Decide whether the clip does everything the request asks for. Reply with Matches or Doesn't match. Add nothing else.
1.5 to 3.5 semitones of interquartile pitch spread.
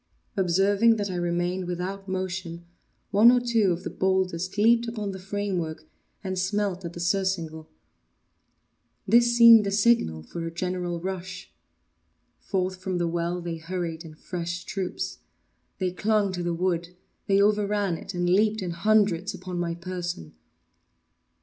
Matches